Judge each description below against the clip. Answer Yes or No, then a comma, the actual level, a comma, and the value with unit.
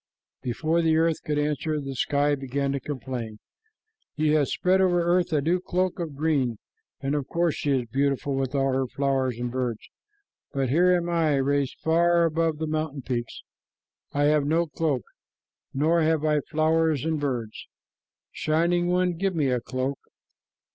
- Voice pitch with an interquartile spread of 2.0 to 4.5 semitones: Yes, average, 3.3 semitones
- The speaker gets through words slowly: No, average, 170 wpm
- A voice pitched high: No, medium, 150 Hz